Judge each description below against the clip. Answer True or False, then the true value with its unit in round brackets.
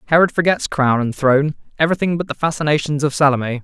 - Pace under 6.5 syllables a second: False (6.9 syllables/s)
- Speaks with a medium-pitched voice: True (150 Hz)